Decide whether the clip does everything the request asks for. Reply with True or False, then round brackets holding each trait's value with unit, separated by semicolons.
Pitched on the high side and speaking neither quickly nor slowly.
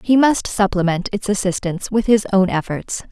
True (200 Hz; 175 wpm)